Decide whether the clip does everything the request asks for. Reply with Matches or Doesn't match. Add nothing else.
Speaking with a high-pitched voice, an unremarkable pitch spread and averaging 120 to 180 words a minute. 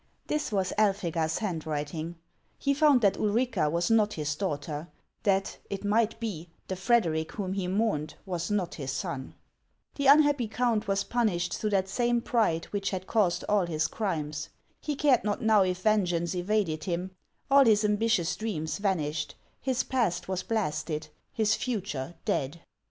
Matches